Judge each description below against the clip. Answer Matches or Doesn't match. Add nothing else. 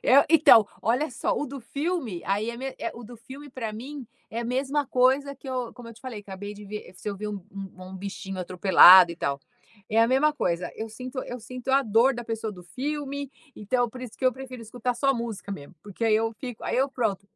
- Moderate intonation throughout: Matches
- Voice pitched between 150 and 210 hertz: Doesn't match